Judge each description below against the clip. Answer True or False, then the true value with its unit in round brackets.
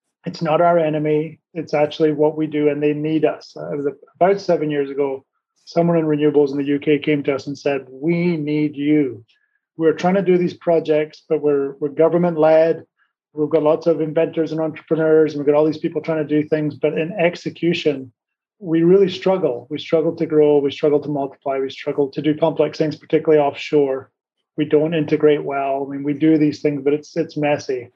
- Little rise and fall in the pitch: True (1.6 semitones)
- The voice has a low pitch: False (150 Hz)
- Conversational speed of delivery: False (210 wpm)